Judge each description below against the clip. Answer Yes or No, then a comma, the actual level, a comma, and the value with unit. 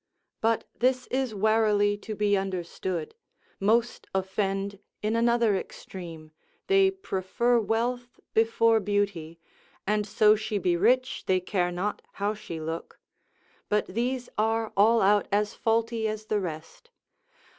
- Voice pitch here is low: No, high, 210 Hz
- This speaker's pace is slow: Yes, slow, 130 wpm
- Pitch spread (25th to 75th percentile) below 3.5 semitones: Yes, average, 3.1 semitones